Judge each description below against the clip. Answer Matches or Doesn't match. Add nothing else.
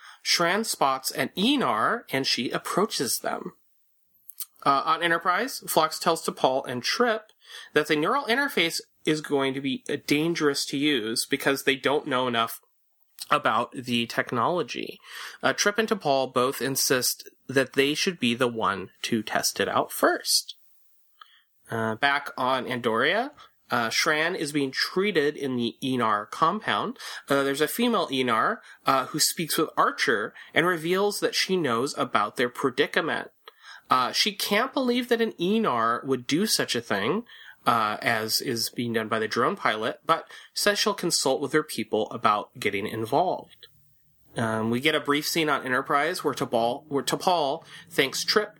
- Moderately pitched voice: Matches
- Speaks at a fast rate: Doesn't match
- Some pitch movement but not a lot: Doesn't match